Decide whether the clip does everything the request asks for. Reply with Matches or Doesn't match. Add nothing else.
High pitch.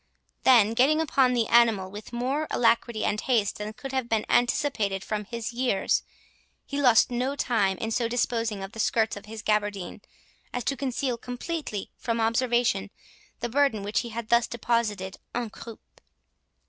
Matches